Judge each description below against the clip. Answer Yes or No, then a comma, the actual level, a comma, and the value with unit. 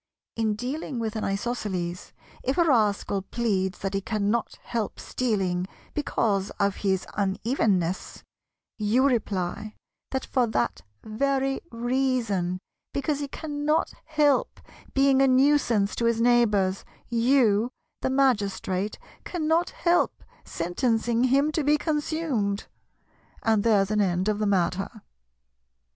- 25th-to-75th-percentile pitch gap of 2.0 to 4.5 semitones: No, average, 5.2 semitones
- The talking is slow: Yes, slow, 120 wpm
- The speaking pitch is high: Yes, high, 230 Hz